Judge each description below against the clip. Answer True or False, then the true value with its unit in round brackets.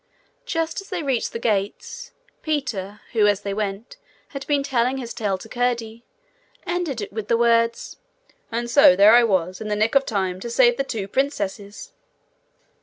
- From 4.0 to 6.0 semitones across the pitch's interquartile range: True (4.8 semitones)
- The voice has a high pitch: True (230 Hz)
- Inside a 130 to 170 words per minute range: False (180 wpm)